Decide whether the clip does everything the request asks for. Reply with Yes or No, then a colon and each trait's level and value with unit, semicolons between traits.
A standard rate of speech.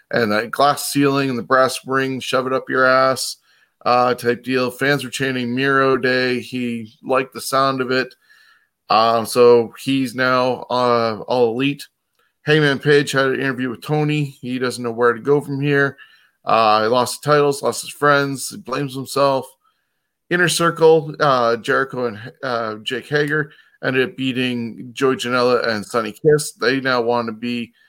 Yes: average, 175 wpm